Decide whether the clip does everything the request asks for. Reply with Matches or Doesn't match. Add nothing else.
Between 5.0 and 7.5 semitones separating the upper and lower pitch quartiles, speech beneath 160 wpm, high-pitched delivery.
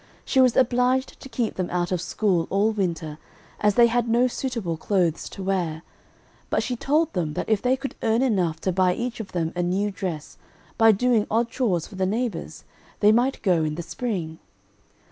Doesn't match